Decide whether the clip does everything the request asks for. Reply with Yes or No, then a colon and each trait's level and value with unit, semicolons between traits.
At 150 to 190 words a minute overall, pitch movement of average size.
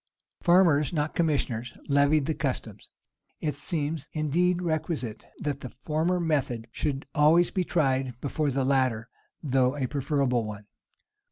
No: slow, 135 wpm; average, 3.5 semitones